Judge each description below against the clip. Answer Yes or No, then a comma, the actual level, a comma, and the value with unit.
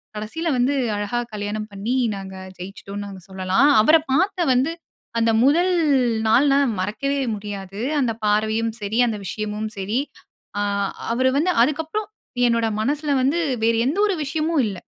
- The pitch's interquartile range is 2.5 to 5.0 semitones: No, wide, 5.6 semitones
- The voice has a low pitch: No, high, 230 Hz